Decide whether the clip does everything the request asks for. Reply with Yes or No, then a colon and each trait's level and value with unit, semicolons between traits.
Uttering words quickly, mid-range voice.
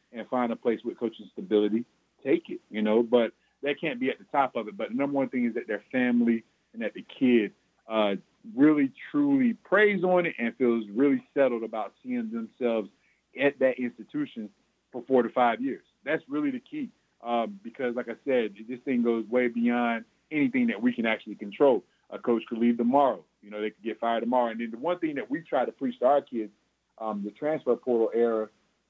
No: fast, 215 wpm; low, 125 Hz